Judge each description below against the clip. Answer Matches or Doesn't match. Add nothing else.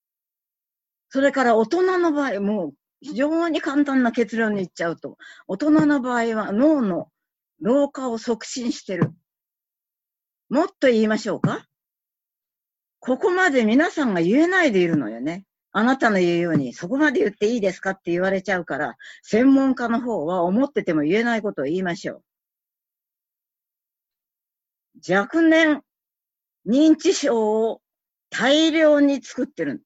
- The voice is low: Doesn't match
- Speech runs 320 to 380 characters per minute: Doesn't match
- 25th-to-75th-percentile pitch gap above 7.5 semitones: Doesn't match